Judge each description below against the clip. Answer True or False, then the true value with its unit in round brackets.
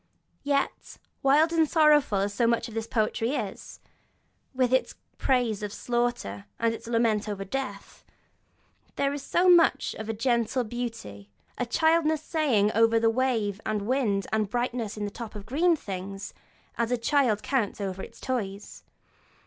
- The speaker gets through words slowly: False (165 wpm)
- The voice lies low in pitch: False (230 Hz)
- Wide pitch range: False (4.3 semitones)